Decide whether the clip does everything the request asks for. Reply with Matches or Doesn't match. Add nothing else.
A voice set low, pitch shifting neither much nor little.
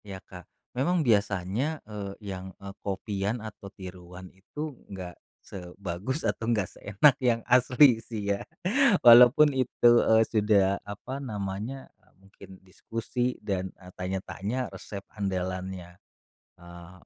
Matches